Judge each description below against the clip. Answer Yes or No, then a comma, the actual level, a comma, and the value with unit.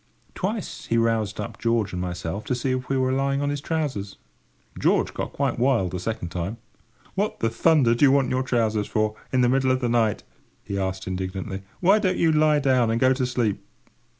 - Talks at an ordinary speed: No, fast, 210 wpm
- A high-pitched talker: No, low, 120 Hz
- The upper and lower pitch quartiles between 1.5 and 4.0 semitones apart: No, average, 4.8 semitones